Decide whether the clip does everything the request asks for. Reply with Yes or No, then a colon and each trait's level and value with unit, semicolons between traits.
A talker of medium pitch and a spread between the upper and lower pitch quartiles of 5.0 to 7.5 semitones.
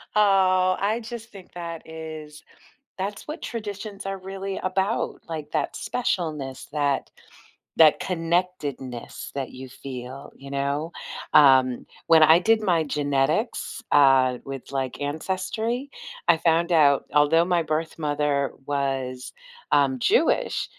Yes: medium, 160 Hz; average, 5.3 semitones